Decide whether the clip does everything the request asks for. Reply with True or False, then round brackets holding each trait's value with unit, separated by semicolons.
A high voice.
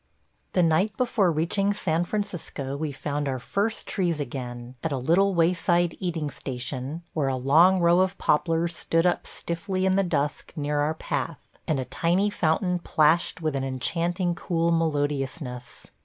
False (165 Hz)